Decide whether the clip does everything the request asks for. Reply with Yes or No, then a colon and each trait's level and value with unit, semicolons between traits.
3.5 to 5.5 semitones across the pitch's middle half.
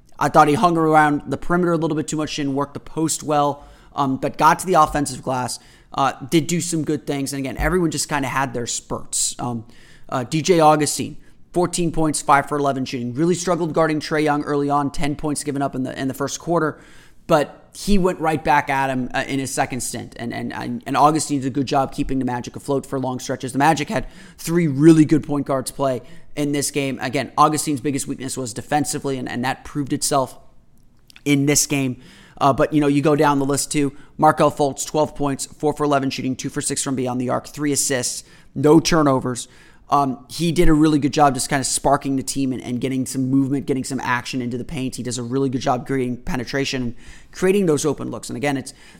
No: narrow, 2.4 semitones